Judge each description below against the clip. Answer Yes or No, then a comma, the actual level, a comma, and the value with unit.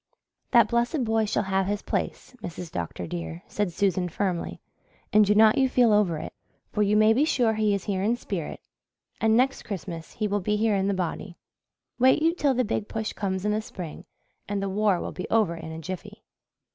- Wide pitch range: No, average, 3.1 semitones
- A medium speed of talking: No, fast, 210 wpm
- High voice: Yes, high, 205 Hz